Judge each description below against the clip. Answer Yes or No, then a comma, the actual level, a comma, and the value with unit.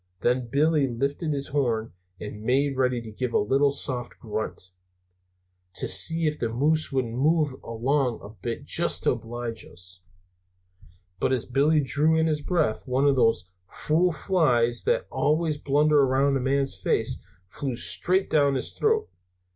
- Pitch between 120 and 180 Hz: Yes, low, 135 Hz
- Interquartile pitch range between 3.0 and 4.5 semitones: Yes, average, 4.0 semitones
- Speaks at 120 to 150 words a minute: No, average, 165 wpm